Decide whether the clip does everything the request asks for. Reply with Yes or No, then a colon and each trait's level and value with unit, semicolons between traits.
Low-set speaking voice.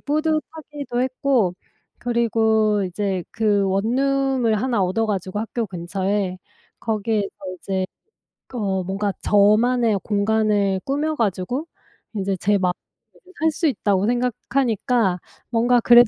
No: high, 220 Hz